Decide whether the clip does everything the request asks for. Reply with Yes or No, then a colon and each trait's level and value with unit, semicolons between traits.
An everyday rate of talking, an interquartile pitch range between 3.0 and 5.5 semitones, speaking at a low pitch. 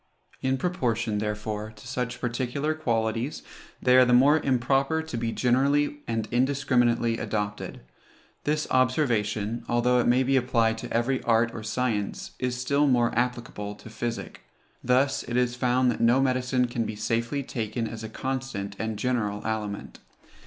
No: average, 155 wpm; narrow, 2.4 semitones; low, 120 Hz